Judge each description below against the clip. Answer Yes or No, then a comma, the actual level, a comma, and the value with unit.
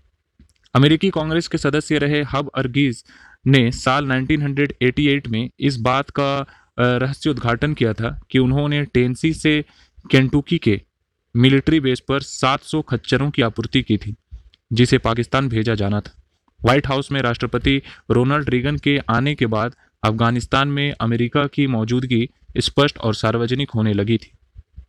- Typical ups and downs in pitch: Yes, average, 3.7 semitones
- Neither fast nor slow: Yes, average, 140 wpm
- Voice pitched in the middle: No, low, 130 Hz